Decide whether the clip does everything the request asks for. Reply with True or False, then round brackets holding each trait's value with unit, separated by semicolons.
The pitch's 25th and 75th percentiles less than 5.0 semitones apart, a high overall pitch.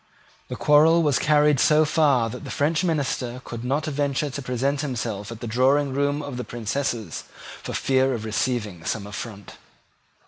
False (3.8 semitones; 130 Hz)